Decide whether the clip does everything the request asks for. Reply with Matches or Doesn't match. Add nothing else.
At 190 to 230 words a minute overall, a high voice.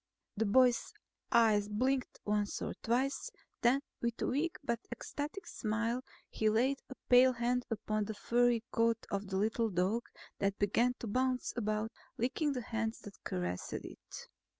Doesn't match